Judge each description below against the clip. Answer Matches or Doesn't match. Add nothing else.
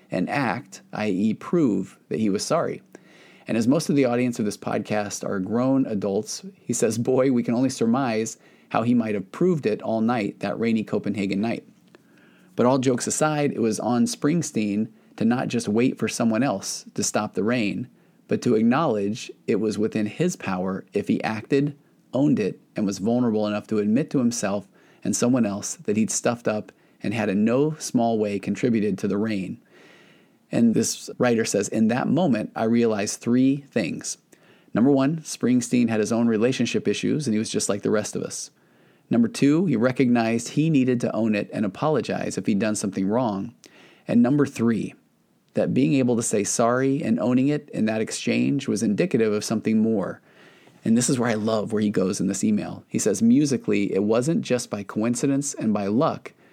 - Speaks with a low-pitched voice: Matches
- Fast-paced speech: Doesn't match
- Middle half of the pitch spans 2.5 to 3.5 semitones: Doesn't match